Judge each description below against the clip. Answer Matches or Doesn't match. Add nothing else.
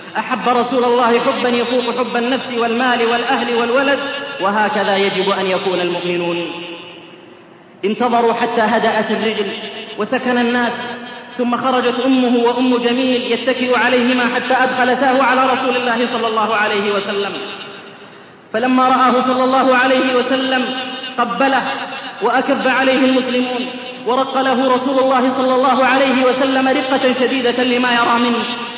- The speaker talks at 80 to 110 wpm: Doesn't match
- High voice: Matches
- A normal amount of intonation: Doesn't match